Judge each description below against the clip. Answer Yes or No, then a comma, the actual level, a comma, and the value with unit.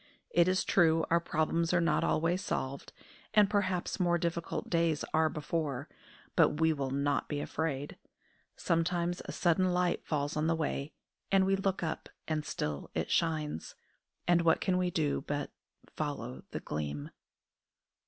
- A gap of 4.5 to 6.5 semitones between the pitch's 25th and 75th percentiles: No, average, 3.0 semitones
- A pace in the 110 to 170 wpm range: Yes, average, 155 wpm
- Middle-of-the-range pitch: Yes, medium, 165 Hz